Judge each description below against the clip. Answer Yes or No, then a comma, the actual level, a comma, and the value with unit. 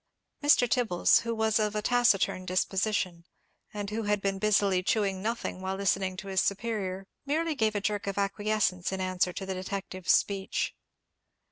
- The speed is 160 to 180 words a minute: Yes, average, 165 wpm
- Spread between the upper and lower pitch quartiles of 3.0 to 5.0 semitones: No, narrow, 2.4 semitones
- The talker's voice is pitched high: Yes, high, 200 Hz